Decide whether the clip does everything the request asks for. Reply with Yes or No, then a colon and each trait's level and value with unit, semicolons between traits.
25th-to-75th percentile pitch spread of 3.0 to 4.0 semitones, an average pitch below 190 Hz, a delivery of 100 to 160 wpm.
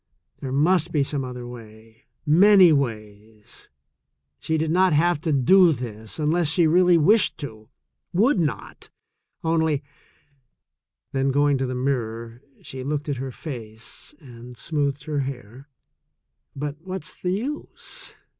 No: average, 5.0 semitones; medium, 140 Hz; average, 145 wpm